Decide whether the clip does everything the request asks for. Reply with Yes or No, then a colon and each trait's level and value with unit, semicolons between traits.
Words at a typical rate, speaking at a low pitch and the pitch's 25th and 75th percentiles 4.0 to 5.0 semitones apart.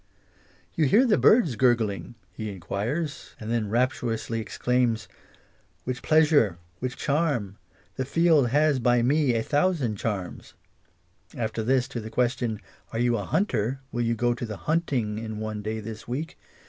Yes: average, 165 wpm; low, 120 Hz; average, 4.3 semitones